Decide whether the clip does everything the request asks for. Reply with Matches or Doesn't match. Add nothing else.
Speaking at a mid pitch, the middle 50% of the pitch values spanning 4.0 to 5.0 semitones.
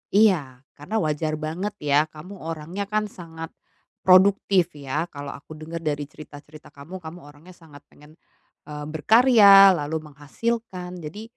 Matches